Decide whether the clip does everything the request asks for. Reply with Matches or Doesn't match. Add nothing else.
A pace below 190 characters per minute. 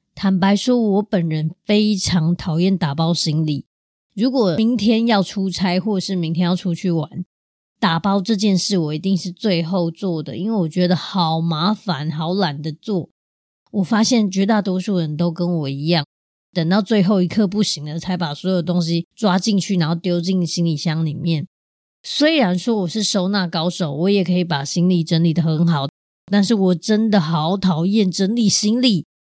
Doesn't match